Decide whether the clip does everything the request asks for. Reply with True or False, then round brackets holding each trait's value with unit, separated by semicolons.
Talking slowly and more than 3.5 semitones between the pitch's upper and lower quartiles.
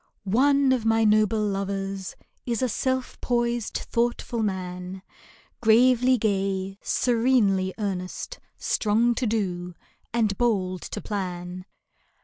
True (110 wpm; 3.9 semitones)